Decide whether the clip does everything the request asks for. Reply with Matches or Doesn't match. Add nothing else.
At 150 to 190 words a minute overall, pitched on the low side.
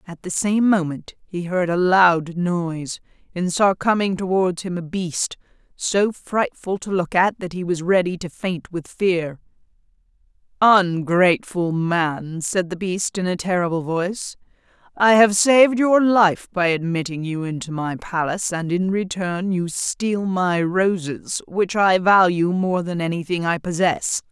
Doesn't match